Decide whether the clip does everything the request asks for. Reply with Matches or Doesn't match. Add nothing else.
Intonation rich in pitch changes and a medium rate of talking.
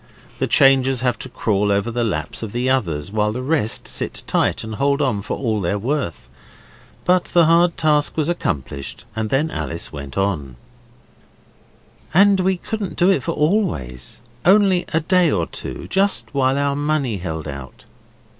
Matches